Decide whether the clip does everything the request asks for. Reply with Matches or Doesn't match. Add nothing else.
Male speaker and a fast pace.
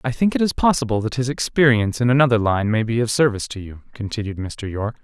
Matches